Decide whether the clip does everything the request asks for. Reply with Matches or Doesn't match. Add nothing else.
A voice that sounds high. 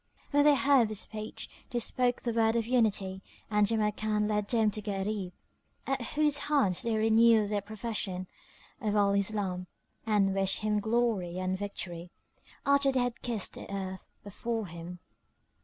Matches